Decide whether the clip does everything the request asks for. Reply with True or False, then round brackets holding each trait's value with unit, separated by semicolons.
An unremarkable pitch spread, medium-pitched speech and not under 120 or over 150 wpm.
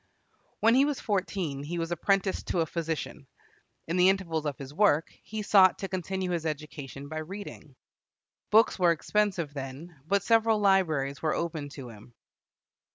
False (4.5 semitones; 170 Hz; 160 wpm)